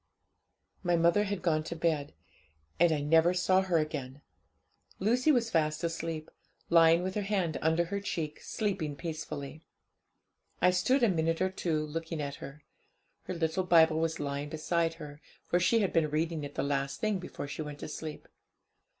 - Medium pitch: Yes, medium, 165 Hz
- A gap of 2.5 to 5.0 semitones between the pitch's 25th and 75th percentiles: Yes, average, 2.9 semitones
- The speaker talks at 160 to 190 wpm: Yes, average, 175 wpm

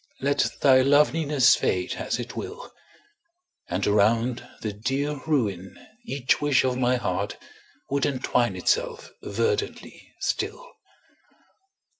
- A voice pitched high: No, low, 130 Hz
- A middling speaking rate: No, slow, 110 wpm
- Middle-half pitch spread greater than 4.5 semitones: No, average, 4.2 semitones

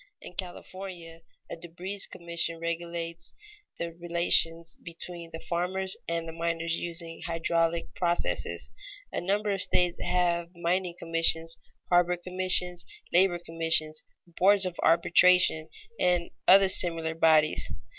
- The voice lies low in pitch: No, medium, 170 Hz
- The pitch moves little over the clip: Yes, narrow, 1.4 semitones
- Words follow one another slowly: Yes, slow, 115 wpm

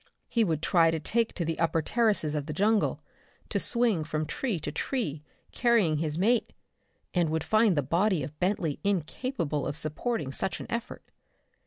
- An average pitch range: No, wide, 6.2 semitones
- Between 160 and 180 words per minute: Yes, average, 175 wpm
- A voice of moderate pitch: Yes, medium, 170 Hz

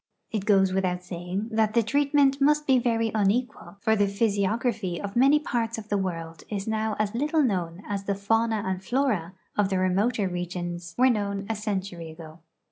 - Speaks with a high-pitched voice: Yes, high, 205 Hz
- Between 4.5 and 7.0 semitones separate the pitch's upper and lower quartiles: No, average, 3.6 semitones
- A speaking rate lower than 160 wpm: No, average, 190 wpm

